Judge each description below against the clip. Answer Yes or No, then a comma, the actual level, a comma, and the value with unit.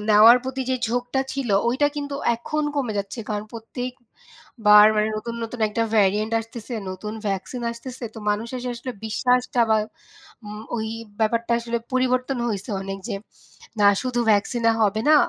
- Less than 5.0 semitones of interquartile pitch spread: Yes, average, 2.8 semitones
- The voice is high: Yes, high, 230 Hz